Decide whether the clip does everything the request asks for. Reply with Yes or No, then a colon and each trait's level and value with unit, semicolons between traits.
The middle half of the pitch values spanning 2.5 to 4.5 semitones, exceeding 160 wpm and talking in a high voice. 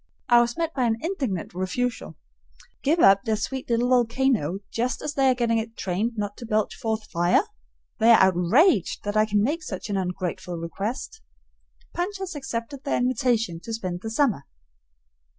No: average, 4.9 semitones; average, 175 wpm; high, 230 Hz